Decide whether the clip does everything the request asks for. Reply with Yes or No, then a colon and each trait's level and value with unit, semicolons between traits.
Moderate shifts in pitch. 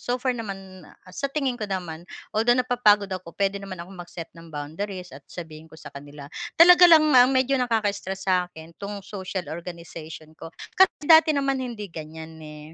No: wide, 6.8 semitones